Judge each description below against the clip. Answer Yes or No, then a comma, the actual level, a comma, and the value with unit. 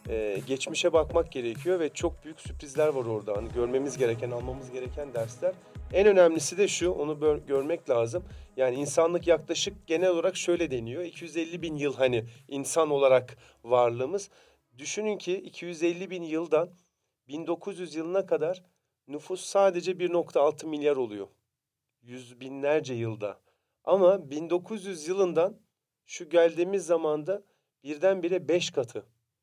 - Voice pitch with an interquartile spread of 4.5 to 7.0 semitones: Yes, average, 5.1 semitones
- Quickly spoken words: No, average, 125 wpm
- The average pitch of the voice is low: No, medium, 160 Hz